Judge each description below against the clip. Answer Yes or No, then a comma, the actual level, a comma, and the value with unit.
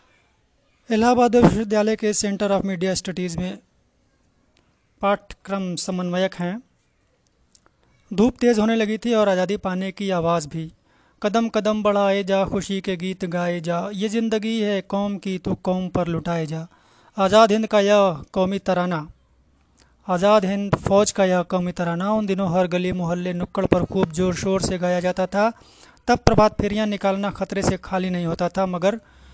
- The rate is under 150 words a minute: No, average, 160 wpm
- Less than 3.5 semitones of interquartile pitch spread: Yes, narrow, 2.5 semitones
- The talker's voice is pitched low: No, high, 190 Hz